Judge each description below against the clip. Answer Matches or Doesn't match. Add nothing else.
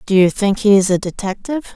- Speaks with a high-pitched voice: Matches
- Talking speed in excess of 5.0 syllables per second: Matches